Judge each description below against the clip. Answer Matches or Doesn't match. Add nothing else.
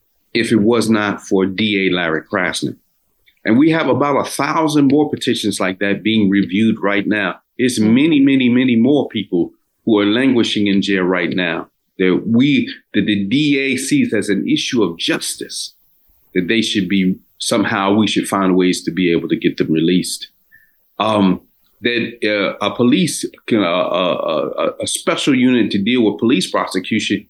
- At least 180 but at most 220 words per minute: Doesn't match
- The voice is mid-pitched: Doesn't match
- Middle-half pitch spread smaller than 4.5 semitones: Doesn't match